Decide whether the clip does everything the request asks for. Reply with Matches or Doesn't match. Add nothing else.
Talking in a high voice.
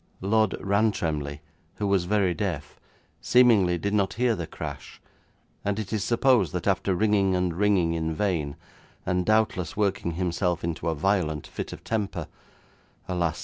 Doesn't match